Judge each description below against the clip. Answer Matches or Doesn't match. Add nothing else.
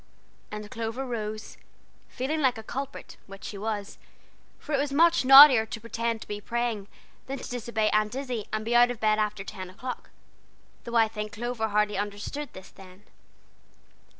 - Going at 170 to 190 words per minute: Matches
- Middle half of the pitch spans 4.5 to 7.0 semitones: Doesn't match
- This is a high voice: Matches